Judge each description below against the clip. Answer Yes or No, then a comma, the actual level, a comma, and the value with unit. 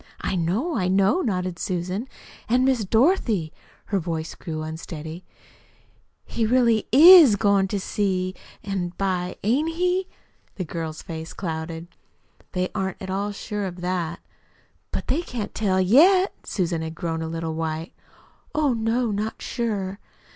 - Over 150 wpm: No, average, 145 wpm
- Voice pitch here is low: No, high, 190 Hz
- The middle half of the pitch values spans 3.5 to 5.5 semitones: Yes, average, 5.1 semitones